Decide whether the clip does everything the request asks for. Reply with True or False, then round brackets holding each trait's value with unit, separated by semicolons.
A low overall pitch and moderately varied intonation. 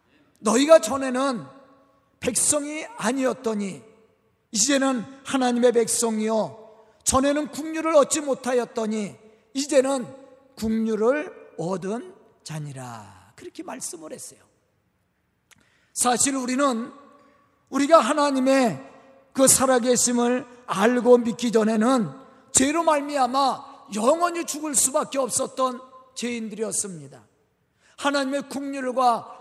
False (255 Hz; 3.7 semitones)